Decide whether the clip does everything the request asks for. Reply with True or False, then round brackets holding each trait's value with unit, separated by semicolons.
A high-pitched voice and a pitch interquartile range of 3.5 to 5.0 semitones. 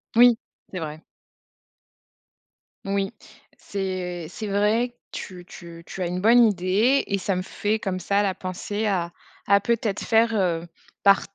False (195 Hz; 2.9 semitones)